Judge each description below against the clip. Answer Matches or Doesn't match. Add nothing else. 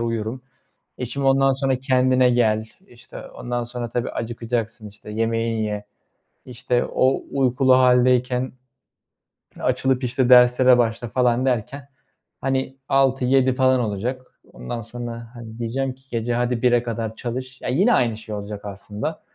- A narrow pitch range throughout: Matches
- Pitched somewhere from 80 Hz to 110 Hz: Doesn't match